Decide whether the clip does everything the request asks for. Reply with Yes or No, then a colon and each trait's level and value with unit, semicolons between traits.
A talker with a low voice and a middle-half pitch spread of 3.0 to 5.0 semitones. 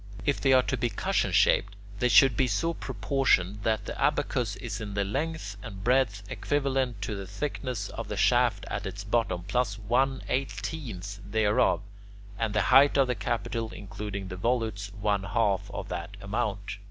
Yes: low, 110 Hz; average, 4.1 semitones